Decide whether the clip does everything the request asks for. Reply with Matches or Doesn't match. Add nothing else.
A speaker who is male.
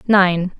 Doesn't match